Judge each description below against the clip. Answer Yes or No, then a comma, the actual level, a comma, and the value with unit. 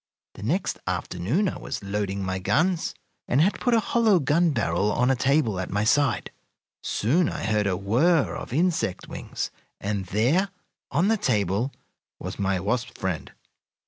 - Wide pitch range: Yes, wide, 9.0 semitones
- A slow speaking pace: No, average, 165 wpm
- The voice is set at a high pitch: No, low, 120 Hz